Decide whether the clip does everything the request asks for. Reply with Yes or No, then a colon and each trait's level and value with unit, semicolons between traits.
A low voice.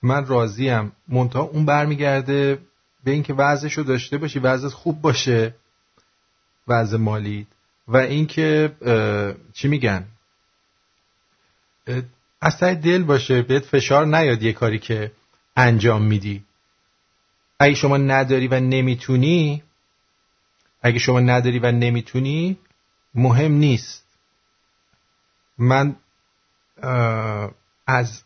Yes: low, 130 Hz